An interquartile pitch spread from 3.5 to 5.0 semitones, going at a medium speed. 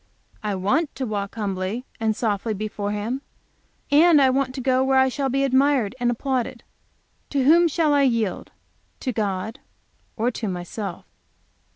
Yes: average, 4.5 semitones; average, 160 wpm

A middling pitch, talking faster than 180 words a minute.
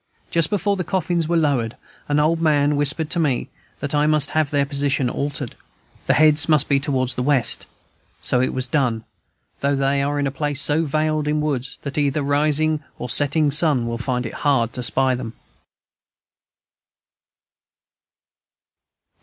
No: medium, 145 Hz; average, 165 wpm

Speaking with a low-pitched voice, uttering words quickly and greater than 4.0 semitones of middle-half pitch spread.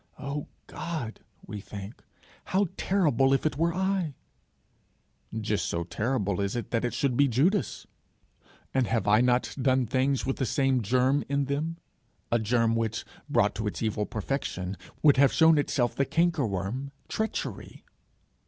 No: low, 130 Hz; average, 155 wpm; average, 4.5 semitones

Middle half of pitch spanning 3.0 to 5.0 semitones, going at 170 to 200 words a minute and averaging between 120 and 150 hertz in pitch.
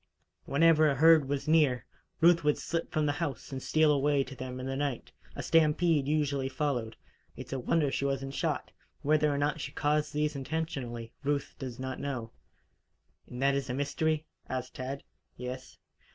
No: narrow, 2.5 semitones; average, 180 wpm; medium, 140 Hz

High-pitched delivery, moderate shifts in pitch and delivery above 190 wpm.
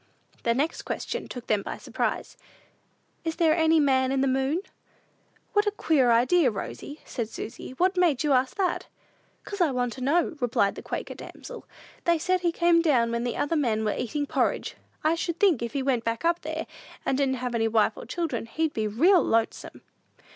No: very high, 275 Hz; wide, 5.8 semitones; average, 200 wpm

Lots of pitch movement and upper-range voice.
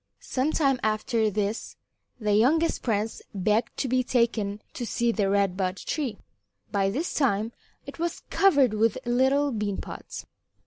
No: average, 4.2 semitones; high, 230 Hz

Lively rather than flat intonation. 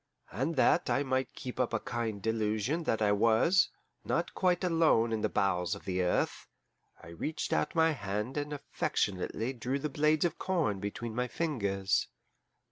Yes: wide, 6.4 semitones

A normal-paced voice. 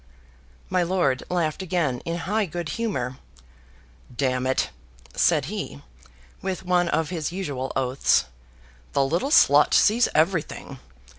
No: slow, 125 wpm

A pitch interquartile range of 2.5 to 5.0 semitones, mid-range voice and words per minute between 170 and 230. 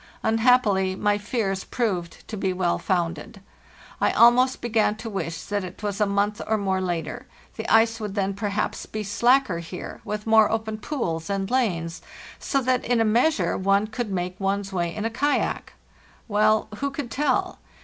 No: average, 3.1 semitones; high, 210 Hz; average, 175 wpm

